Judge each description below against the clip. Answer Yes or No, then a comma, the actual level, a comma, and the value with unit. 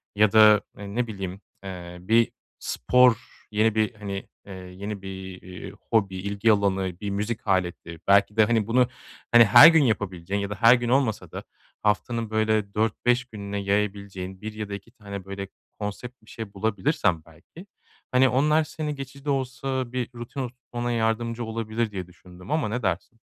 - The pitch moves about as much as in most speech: Yes, average, 3.4 semitones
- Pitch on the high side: No, low, 105 Hz